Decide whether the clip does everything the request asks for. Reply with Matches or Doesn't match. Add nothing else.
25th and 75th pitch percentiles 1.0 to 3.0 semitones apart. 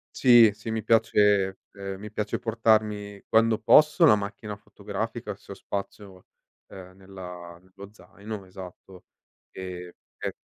Matches